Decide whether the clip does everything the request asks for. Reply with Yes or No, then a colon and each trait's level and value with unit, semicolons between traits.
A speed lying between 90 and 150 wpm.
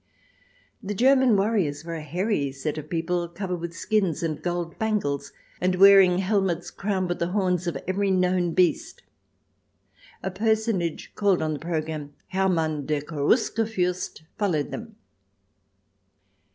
Yes: average, 140 wpm